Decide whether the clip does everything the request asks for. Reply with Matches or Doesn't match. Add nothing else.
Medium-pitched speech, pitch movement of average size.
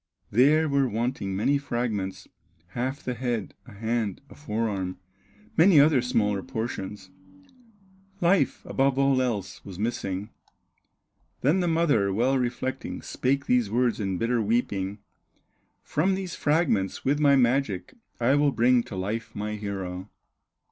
Doesn't match